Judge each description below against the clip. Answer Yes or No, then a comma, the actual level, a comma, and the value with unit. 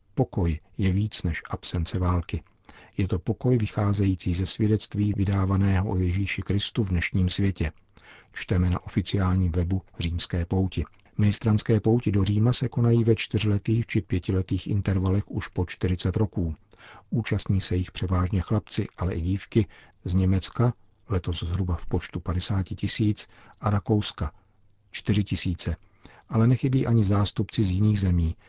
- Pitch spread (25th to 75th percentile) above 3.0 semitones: No, average, 2.7 semitones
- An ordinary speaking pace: Yes, average, 140 wpm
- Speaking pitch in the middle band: No, low, 100 Hz